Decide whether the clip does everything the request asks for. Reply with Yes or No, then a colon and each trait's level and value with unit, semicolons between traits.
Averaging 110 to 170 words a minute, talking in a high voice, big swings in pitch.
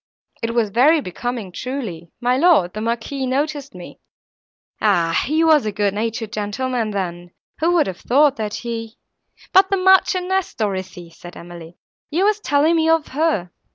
Yes: average, 155 wpm; high, 235 Hz; wide, 7.6 semitones